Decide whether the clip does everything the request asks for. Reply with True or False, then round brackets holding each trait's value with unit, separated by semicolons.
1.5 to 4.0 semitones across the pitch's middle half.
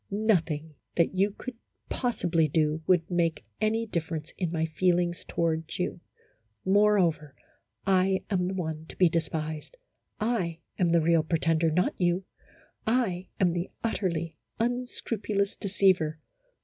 True (3.4 semitones)